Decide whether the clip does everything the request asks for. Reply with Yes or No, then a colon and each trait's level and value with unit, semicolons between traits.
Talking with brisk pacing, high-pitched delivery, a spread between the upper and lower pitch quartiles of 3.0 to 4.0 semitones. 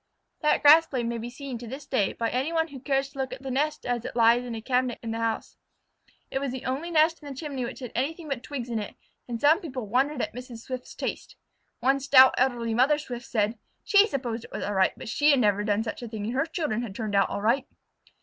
Yes: fast, 265 wpm; very high, 255 Hz; average, 3.3 semitones